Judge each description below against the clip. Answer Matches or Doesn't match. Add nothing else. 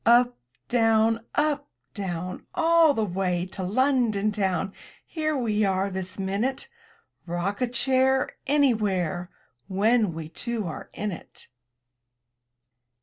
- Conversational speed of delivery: Doesn't match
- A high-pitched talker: Matches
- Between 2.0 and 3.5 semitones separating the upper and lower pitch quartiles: Doesn't match